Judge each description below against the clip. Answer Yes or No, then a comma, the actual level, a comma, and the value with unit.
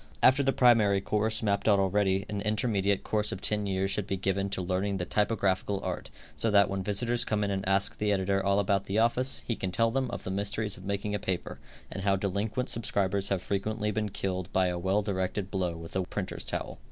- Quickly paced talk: Yes, fast, 225 wpm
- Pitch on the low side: Yes, low, 100 Hz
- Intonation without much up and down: Yes, narrow, 1.8 semitones